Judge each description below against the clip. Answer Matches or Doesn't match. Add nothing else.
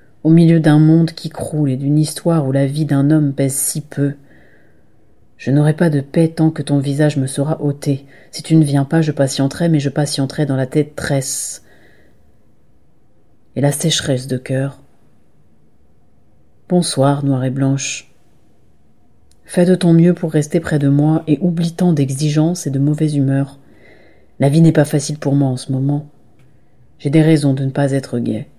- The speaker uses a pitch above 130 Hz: Matches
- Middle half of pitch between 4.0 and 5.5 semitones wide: Doesn't match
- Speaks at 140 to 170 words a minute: Doesn't match